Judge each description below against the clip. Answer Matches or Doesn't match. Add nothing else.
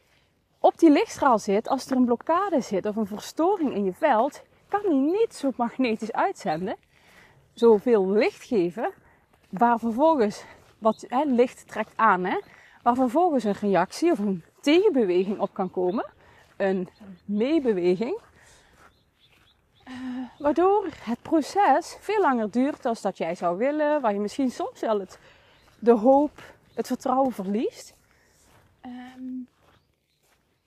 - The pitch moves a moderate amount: Doesn't match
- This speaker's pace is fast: Doesn't match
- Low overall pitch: Doesn't match